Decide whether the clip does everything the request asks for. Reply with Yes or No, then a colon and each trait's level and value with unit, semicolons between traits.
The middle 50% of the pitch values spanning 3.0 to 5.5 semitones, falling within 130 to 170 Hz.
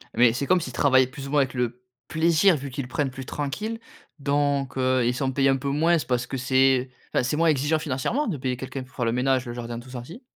No: narrow, 2.5 semitones; low, 135 Hz